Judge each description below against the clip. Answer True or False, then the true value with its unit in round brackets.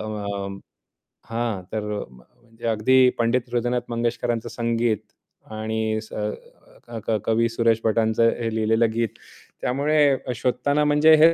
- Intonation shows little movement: True (1.8 semitones)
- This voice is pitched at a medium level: False (115 Hz)